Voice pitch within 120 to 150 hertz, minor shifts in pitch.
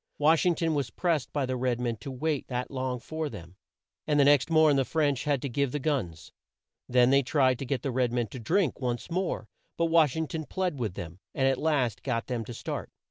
No: low, 135 Hz; average, 3.9 semitones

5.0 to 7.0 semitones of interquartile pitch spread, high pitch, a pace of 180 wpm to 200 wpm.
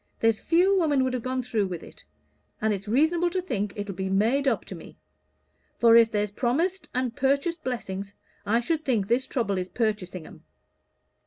Yes: average, 5.3 semitones; high, 235 Hz; average, 185 wpm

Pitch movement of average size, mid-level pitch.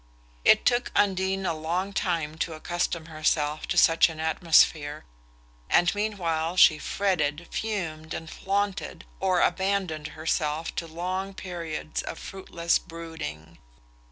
Yes: average, 3.2 semitones; medium, 170 Hz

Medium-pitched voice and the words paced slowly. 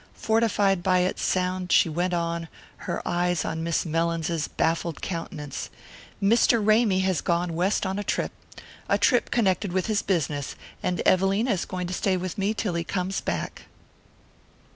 No: medium, 180 Hz; average, 165 wpm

